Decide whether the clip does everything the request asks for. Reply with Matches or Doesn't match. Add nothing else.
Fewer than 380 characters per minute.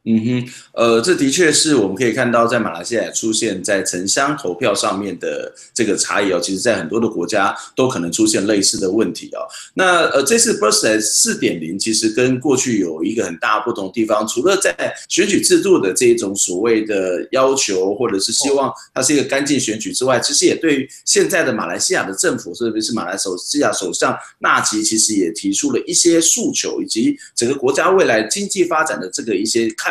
Matches